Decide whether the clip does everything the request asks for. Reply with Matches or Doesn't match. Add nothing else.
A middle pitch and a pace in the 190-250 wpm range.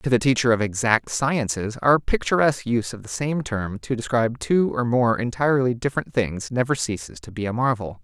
Doesn't match